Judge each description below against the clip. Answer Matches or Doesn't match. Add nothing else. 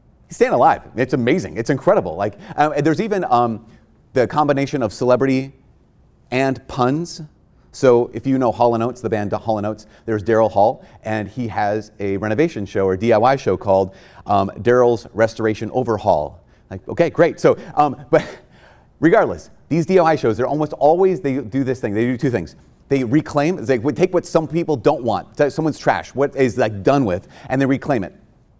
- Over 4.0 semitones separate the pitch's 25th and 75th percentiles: Matches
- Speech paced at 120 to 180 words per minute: Matches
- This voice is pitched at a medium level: Doesn't match